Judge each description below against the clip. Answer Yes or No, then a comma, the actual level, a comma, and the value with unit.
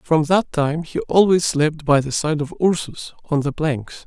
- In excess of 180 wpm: Yes, fast, 205 wpm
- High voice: No, medium, 155 Hz